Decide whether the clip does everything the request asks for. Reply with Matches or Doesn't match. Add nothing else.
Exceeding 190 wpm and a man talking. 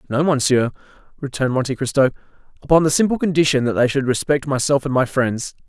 Doesn't match